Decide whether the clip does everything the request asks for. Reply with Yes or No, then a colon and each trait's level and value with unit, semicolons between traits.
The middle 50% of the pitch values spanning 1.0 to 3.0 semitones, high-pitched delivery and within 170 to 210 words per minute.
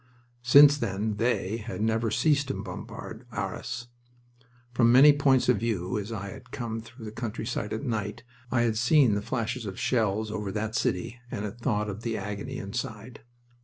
No: average, 2.7 semitones; low, 115 Hz; average, 175 wpm